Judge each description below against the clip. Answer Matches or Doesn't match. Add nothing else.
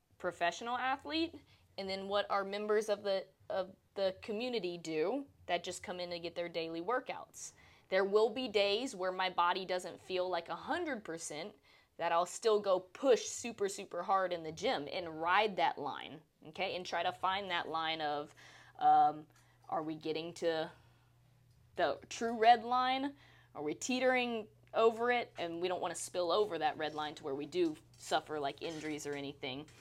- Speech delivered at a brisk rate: Doesn't match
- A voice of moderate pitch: Matches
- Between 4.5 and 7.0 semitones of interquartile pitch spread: Matches